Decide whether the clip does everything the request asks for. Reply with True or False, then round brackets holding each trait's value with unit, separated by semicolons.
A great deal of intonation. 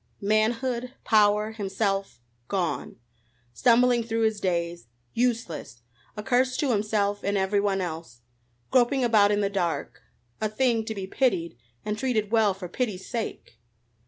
False (3.6 semitones)